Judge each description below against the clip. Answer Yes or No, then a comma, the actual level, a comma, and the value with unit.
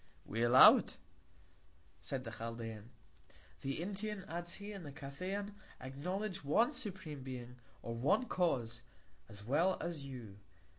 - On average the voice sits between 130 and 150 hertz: Yes, medium, 140 Hz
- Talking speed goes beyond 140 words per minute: No, slow, 135 wpm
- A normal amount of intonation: No, wide, 7.8 semitones